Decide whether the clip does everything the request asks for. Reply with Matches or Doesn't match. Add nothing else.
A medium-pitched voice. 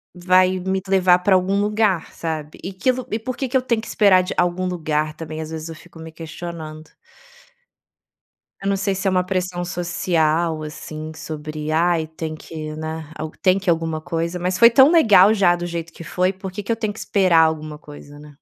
Matches